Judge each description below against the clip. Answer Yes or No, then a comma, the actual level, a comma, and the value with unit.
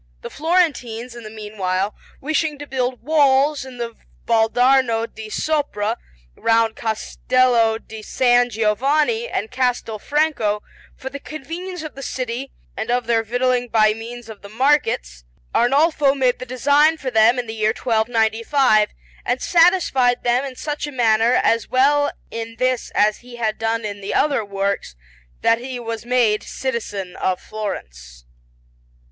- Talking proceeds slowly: No, average, 150 wpm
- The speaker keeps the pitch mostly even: No, average, 3.5 semitones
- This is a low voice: No, high, 240 Hz